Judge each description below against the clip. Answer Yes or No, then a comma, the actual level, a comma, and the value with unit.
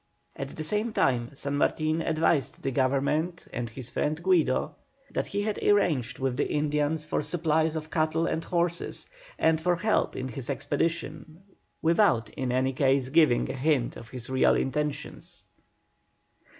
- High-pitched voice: No, medium, 150 Hz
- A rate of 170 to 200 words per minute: No, average, 155 wpm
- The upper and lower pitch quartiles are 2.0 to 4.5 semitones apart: Yes, average, 3.6 semitones